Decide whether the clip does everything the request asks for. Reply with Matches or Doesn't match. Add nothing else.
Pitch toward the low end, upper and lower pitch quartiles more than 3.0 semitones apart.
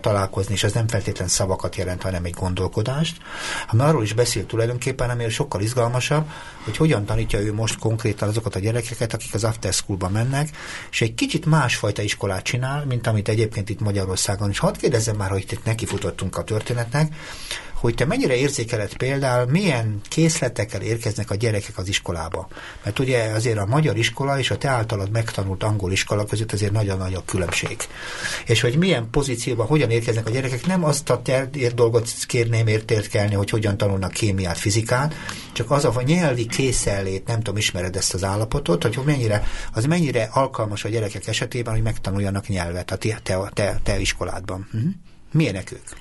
Matches